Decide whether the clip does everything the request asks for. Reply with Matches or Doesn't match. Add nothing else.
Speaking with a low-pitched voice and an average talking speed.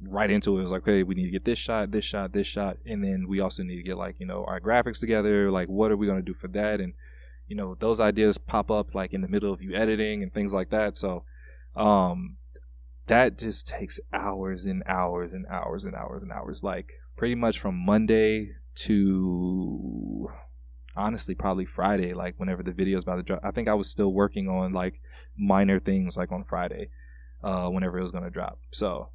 Doesn't match